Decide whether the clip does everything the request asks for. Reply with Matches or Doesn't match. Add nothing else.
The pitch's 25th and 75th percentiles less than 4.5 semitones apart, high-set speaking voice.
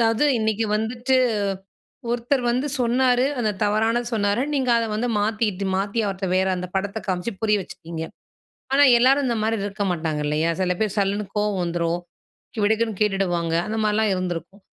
Matches